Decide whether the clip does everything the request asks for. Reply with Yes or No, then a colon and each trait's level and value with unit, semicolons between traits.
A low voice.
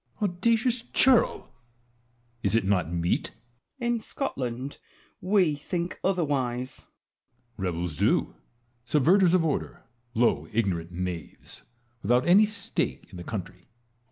Yes: low, 130 Hz